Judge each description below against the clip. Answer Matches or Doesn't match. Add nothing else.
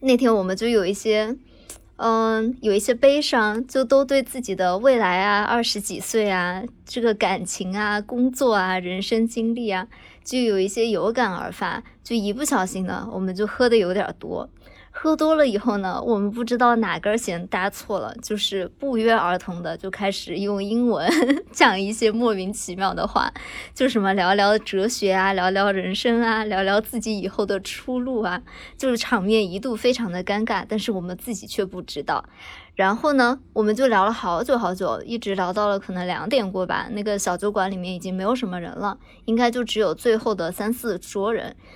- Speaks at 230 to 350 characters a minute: Matches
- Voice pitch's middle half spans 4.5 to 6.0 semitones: Doesn't match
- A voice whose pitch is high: Matches